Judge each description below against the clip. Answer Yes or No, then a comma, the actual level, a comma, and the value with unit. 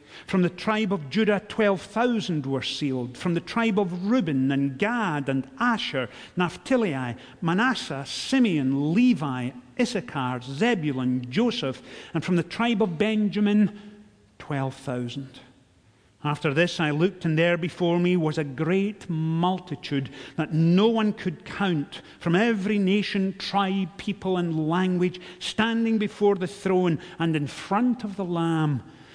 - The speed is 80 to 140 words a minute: Yes, slow, 135 wpm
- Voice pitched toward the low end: No, medium, 175 Hz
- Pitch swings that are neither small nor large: No, wide, 6.3 semitones